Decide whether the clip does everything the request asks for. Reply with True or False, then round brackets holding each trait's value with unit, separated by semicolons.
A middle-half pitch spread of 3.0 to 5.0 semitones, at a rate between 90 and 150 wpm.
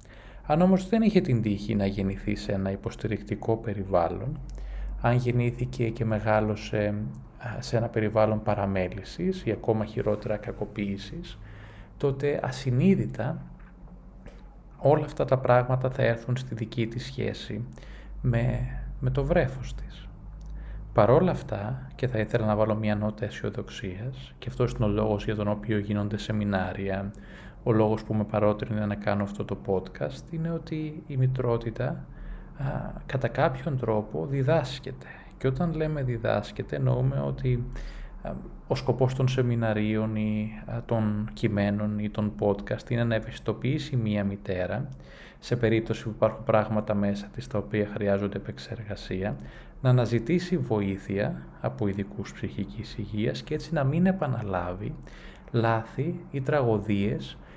True (3.7 semitones; 130 wpm)